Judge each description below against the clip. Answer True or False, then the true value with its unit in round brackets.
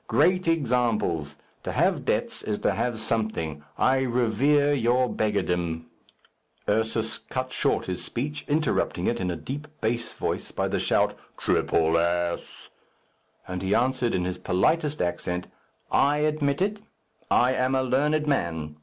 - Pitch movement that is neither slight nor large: False (7.7 semitones)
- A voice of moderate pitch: False (120 Hz)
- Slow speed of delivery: False (145 wpm)